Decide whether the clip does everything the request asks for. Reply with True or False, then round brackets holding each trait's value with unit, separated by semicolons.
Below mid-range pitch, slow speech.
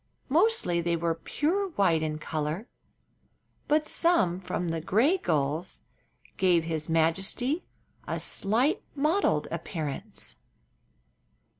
False (180 Hz; 105 wpm)